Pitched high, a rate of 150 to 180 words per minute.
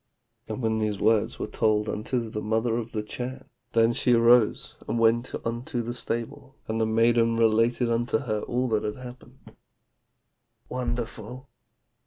No: low, 115 Hz; average, 155 wpm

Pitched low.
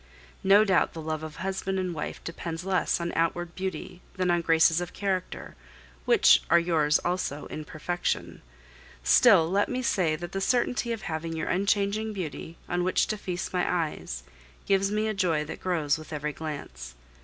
No: medium, 175 Hz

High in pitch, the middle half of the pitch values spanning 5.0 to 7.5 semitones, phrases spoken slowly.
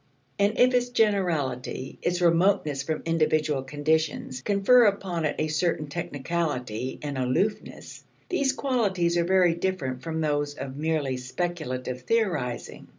No: medium, 160 Hz; average, 5.3 semitones; slow, 130 wpm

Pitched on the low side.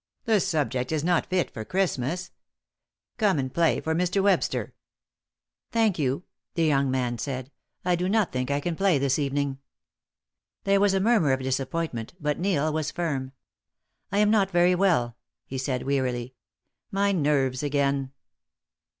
No: medium, 150 Hz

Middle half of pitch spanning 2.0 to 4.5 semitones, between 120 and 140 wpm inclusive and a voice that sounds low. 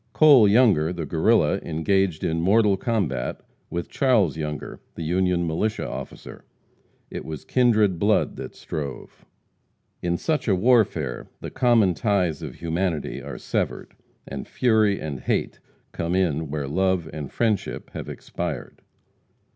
No: average, 5.2 semitones; slow, 135 wpm; very low, 90 Hz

